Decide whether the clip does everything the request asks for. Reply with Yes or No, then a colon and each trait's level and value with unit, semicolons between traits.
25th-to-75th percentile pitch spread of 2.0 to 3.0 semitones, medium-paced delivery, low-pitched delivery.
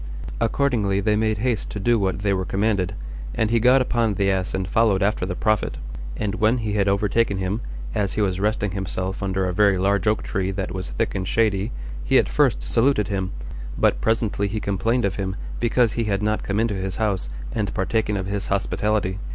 No: narrow, 2.4 semitones; fast, 210 wpm; low, 100 Hz